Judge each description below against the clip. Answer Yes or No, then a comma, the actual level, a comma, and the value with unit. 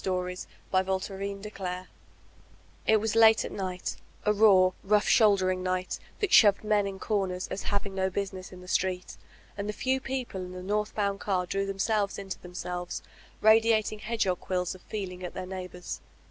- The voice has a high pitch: Yes, high, 195 Hz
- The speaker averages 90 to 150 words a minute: No, average, 170 wpm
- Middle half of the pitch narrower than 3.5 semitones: Yes, narrow, 2.4 semitones